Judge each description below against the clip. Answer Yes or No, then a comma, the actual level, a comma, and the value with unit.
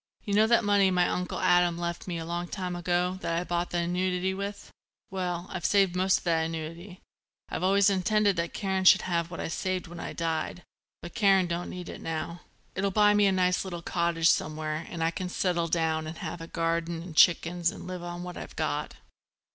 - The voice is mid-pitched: Yes, medium, 175 Hz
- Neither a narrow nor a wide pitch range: No, narrow, 1.9 semitones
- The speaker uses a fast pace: Yes, fast, 215 wpm